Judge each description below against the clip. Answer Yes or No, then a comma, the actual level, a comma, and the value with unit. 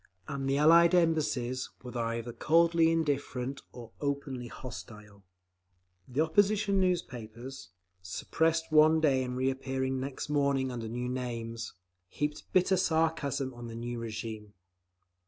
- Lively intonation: No, average, 4.8 semitones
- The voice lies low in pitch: Yes, low, 130 Hz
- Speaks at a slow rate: Yes, slow, 120 wpm